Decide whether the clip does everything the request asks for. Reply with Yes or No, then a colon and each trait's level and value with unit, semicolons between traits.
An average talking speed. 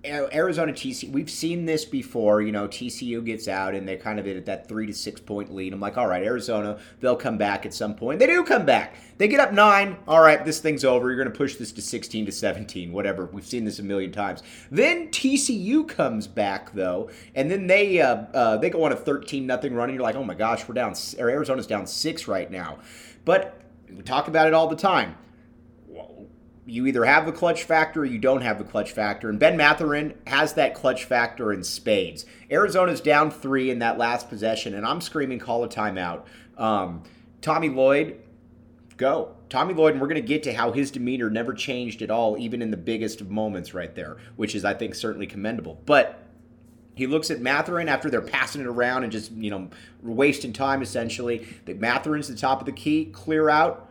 No: fast, 215 wpm